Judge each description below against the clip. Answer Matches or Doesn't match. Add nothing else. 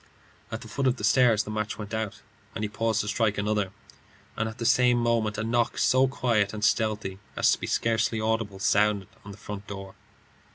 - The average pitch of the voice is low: Matches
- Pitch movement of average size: Doesn't match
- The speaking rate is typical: Doesn't match